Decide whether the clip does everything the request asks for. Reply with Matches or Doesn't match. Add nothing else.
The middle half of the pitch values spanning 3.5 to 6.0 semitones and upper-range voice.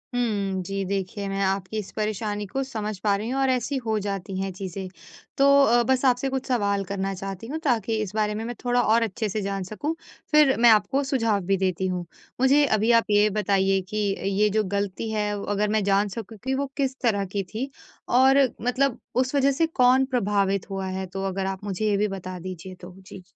Matches